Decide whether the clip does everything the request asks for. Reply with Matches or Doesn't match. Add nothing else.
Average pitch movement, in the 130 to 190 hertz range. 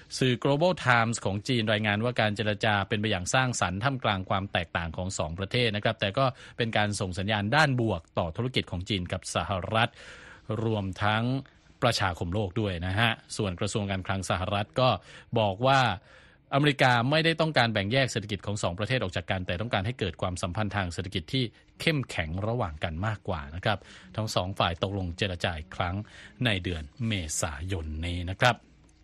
Doesn't match